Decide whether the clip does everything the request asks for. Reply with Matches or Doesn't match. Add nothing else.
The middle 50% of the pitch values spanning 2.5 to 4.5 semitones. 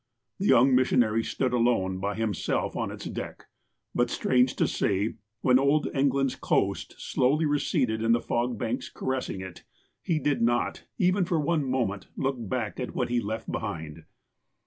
Matches